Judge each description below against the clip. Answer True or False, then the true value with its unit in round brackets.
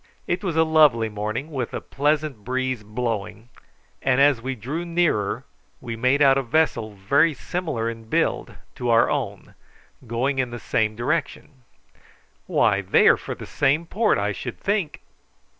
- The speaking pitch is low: True (130 Hz)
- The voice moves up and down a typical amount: True (4.9 semitones)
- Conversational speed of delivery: True (160 wpm)